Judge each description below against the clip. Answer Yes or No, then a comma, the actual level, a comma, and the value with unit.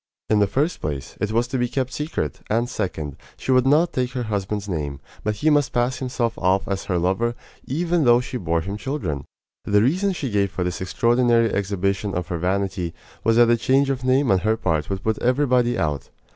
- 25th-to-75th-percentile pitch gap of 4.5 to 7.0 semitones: Yes, average, 5.2 semitones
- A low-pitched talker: Yes, low, 110 Hz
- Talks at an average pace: No, fast, 215 wpm